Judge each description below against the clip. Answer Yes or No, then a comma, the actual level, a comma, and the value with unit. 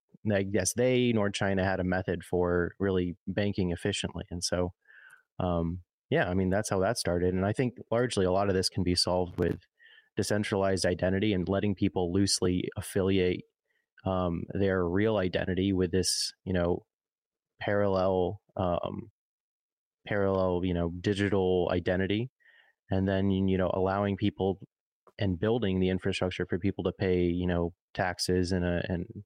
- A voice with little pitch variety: Yes, narrow, 1.8 semitones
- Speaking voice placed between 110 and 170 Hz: No, very low, 95 Hz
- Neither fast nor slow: Yes, average, 155 wpm